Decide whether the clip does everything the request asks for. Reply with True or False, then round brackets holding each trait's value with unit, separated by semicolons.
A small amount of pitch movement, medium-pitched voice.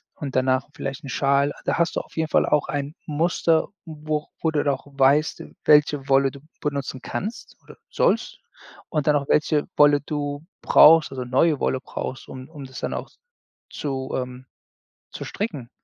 True (2.1 semitones; 145 Hz)